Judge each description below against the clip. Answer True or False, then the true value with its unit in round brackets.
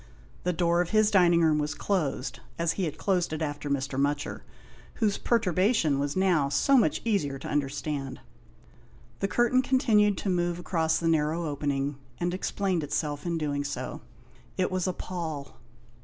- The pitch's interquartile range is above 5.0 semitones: False (4.4 semitones)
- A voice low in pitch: False (165 Hz)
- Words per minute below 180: True (165 wpm)